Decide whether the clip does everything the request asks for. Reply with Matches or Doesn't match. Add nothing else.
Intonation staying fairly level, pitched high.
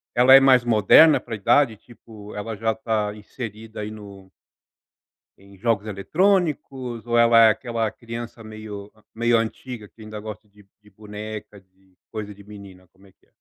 Doesn't match